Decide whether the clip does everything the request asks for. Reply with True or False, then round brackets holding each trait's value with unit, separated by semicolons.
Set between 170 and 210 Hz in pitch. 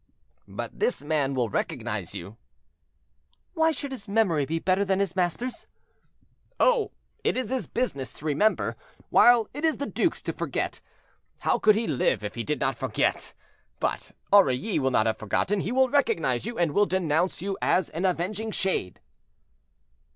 True (190 Hz)